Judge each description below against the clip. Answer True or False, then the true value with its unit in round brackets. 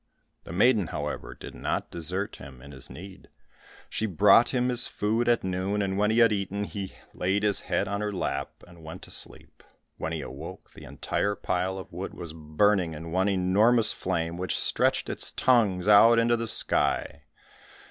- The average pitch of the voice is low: True (100 Hz)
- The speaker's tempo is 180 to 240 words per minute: True (185 wpm)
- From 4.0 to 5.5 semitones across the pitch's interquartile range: False (3.0 semitones)